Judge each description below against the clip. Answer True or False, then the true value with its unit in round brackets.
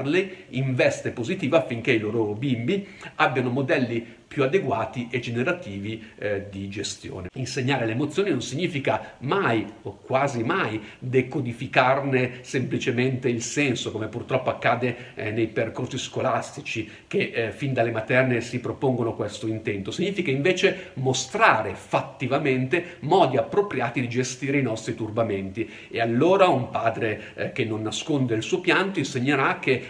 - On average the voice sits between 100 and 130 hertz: True (125 Hz)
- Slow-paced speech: False (140 wpm)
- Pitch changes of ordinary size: True (3.7 semitones)